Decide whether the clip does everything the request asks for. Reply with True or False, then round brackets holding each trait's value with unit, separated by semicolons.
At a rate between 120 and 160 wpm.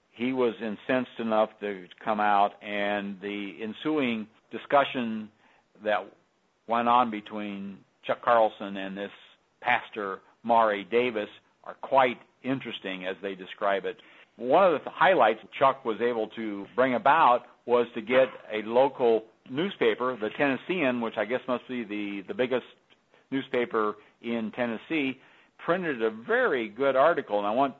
True (140 wpm)